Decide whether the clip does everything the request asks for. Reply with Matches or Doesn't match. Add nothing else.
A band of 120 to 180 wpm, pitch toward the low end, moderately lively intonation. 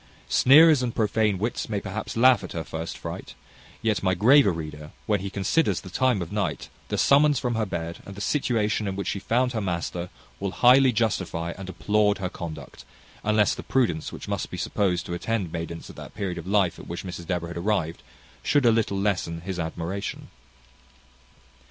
Doesn't match